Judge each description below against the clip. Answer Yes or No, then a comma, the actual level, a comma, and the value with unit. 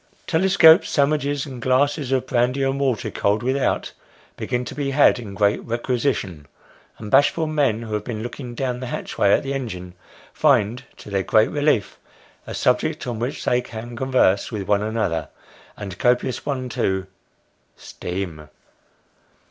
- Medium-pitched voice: No, low, 125 Hz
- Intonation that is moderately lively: Yes, average, 4.5 semitones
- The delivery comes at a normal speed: Yes, average, 155 wpm